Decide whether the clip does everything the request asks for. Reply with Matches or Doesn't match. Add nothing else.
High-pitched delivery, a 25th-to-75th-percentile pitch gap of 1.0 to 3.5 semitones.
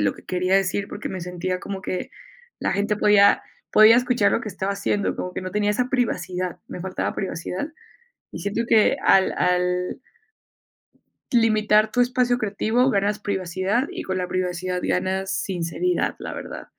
Matches